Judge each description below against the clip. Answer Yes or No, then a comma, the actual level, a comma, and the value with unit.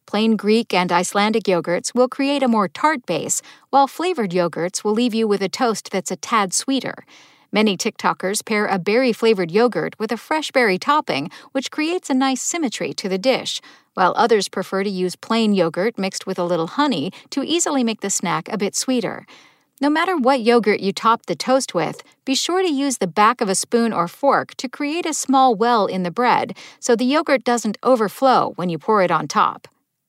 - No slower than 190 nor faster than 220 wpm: Yes, fast, 205 wpm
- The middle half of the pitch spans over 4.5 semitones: Yes, wide, 5.6 semitones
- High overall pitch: Yes, high, 230 Hz